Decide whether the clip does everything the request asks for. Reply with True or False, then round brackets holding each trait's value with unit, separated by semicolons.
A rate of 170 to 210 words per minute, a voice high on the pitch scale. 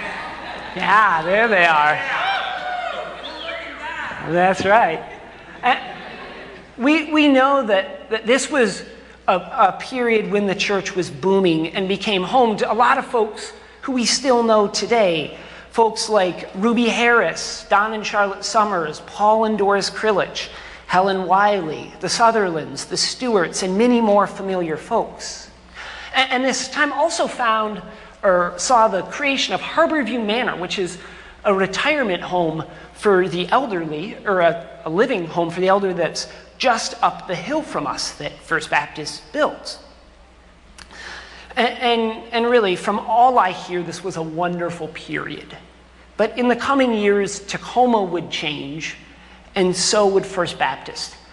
False (145 wpm; 205 Hz)